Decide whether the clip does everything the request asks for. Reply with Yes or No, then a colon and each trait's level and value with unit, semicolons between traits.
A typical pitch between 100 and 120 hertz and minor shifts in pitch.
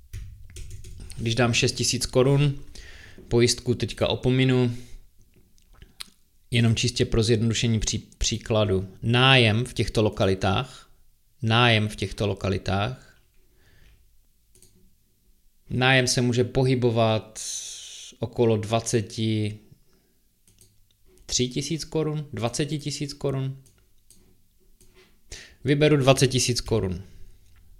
No: low, 115 Hz; average, 4.2 semitones